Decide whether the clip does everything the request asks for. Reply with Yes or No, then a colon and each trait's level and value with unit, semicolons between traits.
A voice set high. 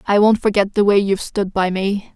Yes: high, 200 Hz